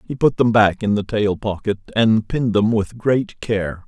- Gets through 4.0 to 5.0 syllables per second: Yes, 4.5 syllables/s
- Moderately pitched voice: No, low, 110 Hz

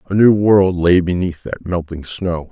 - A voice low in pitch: Yes, very low, 90 Hz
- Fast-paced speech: No, average, 190 wpm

